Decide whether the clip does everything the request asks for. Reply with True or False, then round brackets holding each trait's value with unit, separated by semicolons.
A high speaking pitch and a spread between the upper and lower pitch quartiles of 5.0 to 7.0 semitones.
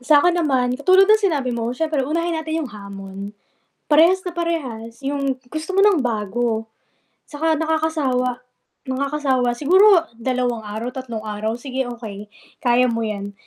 True (260 Hz; 5.5 semitones)